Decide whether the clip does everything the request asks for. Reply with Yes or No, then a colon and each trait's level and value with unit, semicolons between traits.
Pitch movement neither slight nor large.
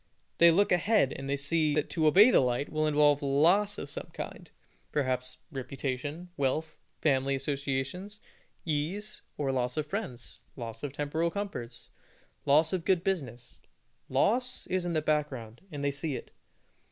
Yes: average, 4.2 semitones